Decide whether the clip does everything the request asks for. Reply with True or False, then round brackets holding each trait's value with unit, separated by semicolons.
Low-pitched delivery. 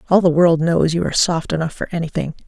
False (165 Hz)